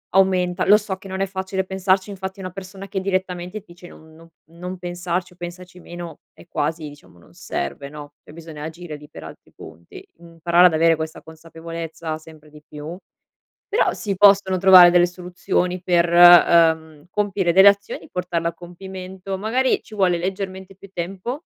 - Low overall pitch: No, medium, 180 Hz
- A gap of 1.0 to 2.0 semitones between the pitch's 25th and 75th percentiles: No, narrow, 2.5 semitones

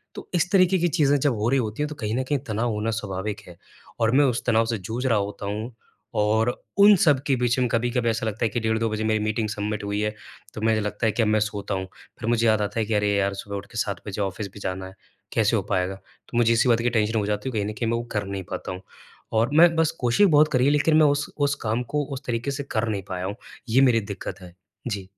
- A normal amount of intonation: Yes, average, 3.5 semitones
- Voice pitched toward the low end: Yes, low, 110 Hz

